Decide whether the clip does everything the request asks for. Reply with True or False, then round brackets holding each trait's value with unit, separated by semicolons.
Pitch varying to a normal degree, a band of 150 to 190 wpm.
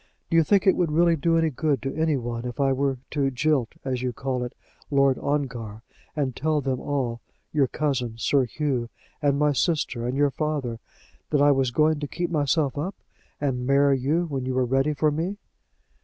False (3.1 semitones; 200 wpm)